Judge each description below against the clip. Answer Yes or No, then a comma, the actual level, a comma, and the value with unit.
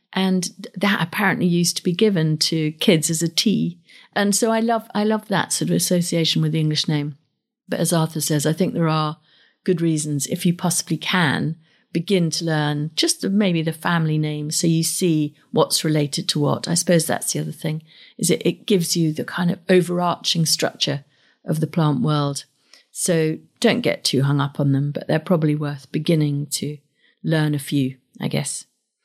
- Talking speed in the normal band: Yes, average, 195 wpm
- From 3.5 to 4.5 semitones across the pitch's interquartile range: No, average, 3.0 semitones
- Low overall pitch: No, medium, 165 Hz